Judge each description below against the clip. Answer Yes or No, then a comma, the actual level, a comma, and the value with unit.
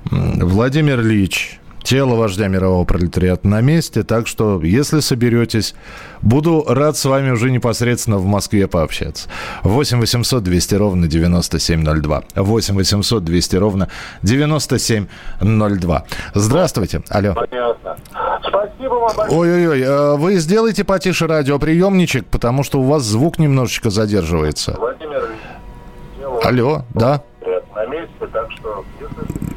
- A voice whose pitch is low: Yes, low, 115 Hz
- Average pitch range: No, wide, 7.2 semitones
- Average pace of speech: No, slow, 95 wpm